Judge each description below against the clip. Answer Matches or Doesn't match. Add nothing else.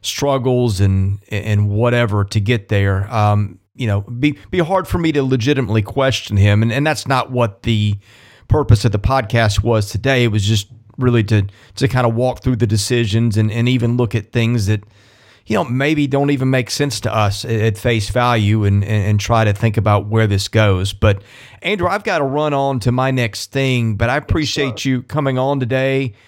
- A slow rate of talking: Doesn't match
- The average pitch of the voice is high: Doesn't match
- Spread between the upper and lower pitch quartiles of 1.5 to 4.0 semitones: Matches